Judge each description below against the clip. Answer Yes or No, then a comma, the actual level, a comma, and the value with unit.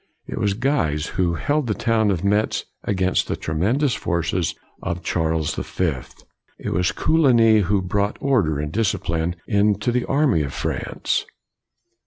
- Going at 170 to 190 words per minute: No, average, 155 wpm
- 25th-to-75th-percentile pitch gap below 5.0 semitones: No, wide, 5.5 semitones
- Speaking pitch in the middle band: No, low, 100 Hz